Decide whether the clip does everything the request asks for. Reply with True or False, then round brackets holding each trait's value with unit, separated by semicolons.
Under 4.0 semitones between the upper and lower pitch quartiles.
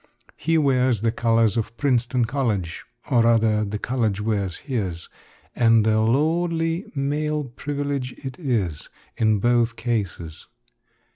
False (4.3 semitones)